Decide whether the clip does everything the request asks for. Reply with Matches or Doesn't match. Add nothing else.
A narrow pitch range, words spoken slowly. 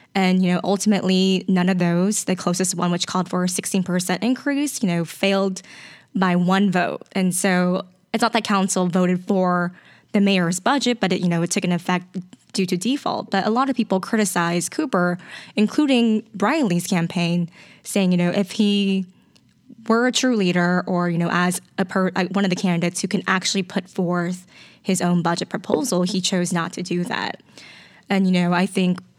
Doesn't match